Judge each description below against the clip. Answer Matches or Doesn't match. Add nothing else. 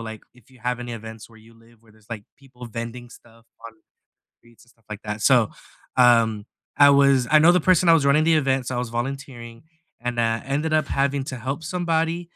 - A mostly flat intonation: Doesn't match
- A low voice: Matches